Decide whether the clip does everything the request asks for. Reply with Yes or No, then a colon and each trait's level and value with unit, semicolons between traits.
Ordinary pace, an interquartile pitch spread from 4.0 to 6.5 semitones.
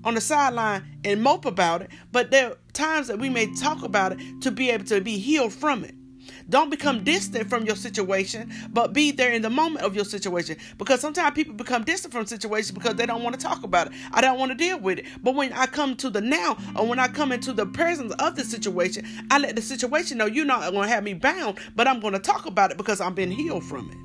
No: fast, 255 wpm; average, 5.0 semitones